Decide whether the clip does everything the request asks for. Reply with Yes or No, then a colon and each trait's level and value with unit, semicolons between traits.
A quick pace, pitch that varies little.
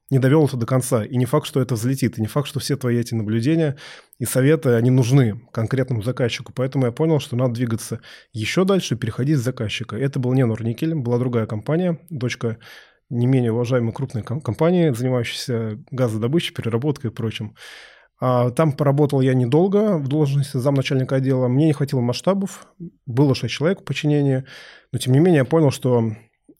No: fast, 180 wpm; average, 3.6 semitones